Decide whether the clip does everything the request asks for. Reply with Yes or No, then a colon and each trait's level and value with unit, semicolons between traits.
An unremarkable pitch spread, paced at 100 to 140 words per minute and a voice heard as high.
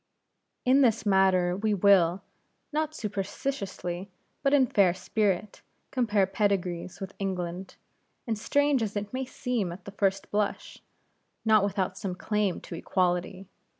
Yes: average, 3.0 semitones; slow, 135 wpm; high, 200 Hz